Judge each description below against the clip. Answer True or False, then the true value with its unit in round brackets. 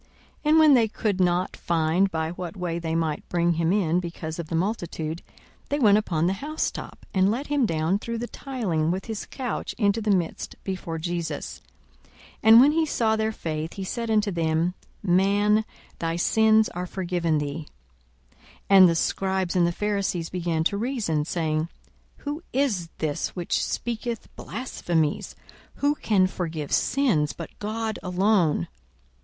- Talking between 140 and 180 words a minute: True (165 wpm)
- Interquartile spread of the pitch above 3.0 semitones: True (4.8 semitones)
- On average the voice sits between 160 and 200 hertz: True (185 Hz)